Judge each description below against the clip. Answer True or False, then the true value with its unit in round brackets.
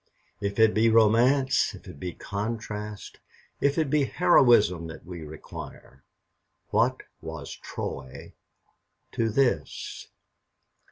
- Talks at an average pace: False (110 wpm)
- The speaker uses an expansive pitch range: True (6.1 semitones)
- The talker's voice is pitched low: True (110 Hz)